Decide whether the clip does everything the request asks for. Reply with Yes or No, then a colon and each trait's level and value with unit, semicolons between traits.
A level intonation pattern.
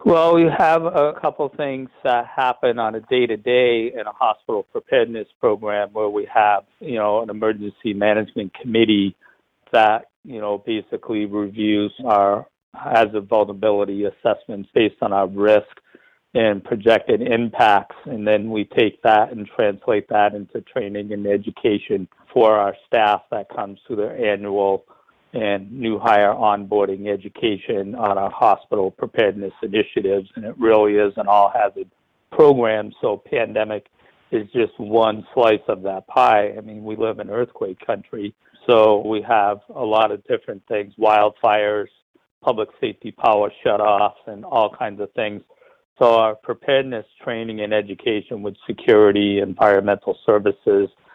Yes: narrow, 2.0 semitones